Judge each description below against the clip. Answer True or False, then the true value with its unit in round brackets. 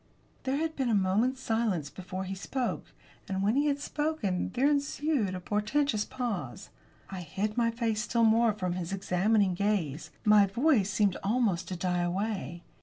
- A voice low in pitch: False (210 Hz)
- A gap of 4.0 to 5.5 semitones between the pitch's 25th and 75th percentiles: True (4.6 semitones)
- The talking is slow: False (170 wpm)